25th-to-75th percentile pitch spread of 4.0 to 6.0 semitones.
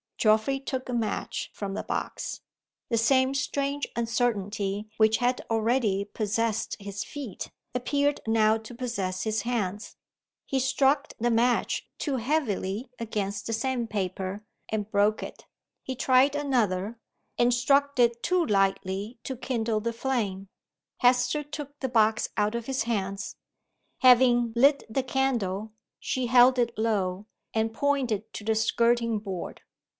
No: average, 3.5 semitones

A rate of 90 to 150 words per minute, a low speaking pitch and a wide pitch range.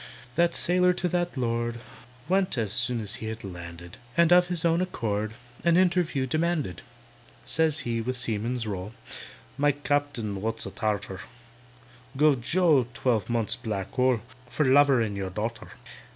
Yes: average, 145 wpm; low, 125 Hz; wide, 6.7 semitones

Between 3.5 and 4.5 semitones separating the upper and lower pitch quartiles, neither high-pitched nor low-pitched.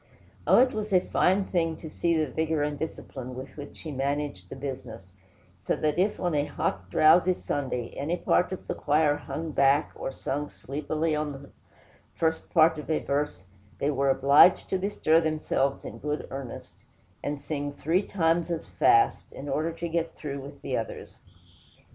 No: average, 2.9 semitones; medium, 150 Hz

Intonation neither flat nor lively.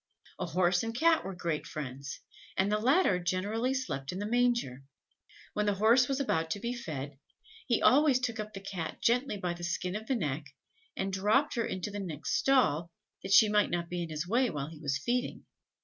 No: wide, 6.3 semitones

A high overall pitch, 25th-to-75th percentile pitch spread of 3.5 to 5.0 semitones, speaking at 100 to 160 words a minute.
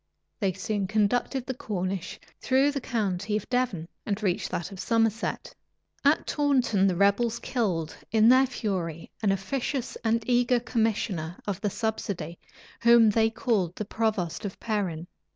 Yes: high, 215 Hz; average, 3.8 semitones; average, 150 wpm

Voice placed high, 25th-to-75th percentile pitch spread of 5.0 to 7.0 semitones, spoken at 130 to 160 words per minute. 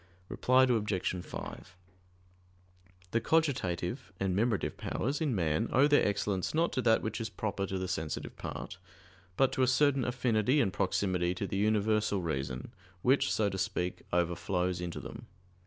No: low, 105 Hz; wide, 5.5 semitones; average, 155 wpm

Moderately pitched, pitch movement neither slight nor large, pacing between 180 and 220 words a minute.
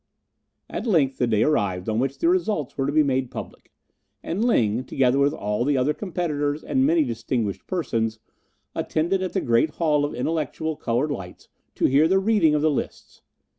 Yes: medium, 145 Hz; average, 4.9 semitones; average, 185 wpm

